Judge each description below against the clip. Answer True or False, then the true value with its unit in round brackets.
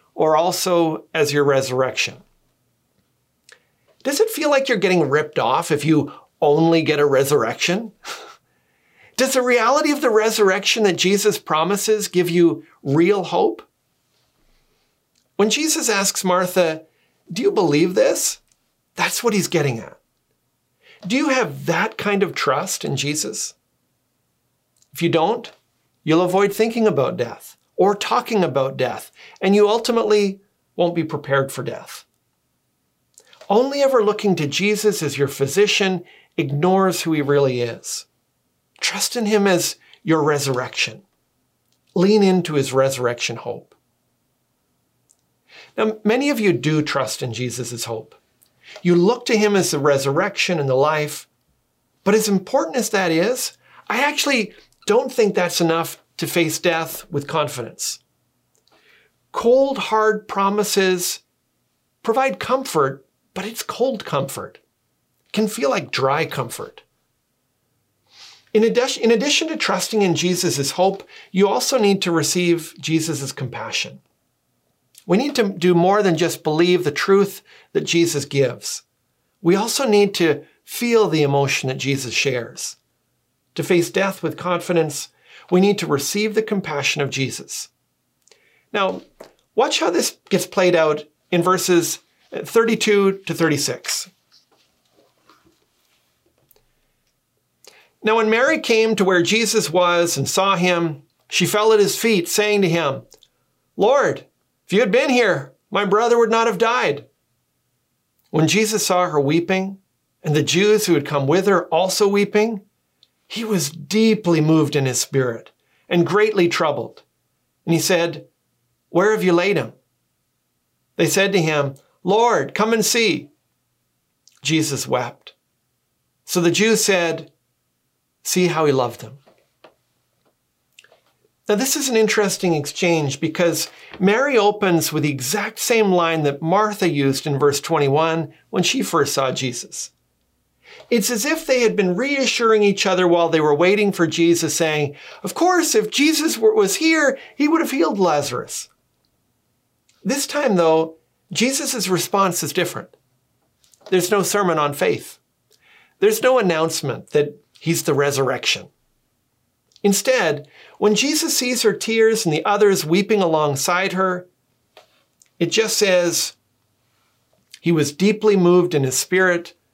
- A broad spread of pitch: True (5.9 semitones)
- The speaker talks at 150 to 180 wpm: False (135 wpm)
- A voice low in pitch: False (180 Hz)